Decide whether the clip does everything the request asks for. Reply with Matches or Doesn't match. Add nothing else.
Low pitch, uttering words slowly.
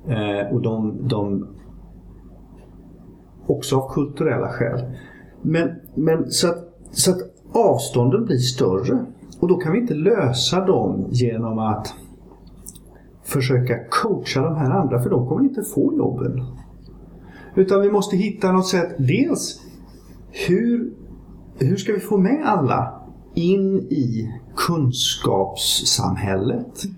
Matches